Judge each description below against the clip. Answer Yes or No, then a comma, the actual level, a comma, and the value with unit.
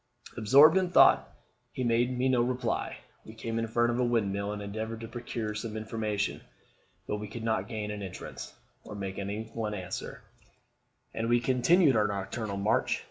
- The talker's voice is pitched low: Yes, low, 110 Hz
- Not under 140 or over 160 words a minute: No, average, 180 wpm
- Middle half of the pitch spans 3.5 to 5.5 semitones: No, narrow, 2.4 semitones